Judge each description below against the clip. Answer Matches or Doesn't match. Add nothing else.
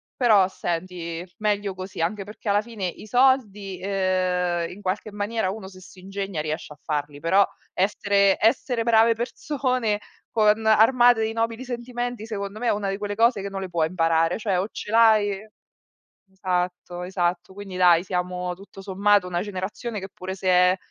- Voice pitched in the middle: Doesn't match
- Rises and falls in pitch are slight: Doesn't match